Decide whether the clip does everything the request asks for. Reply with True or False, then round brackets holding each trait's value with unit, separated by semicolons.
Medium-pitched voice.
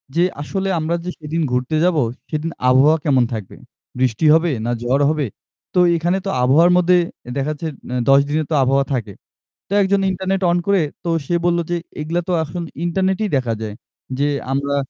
True (155 Hz)